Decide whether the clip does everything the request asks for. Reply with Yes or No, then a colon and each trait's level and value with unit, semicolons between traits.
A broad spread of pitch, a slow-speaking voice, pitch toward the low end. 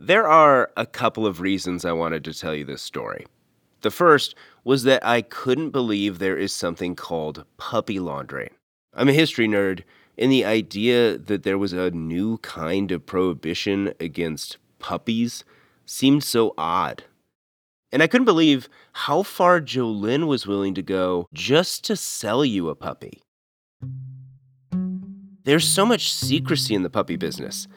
No: wide, 6.9 semitones; average, 155 wpm; low, 110 Hz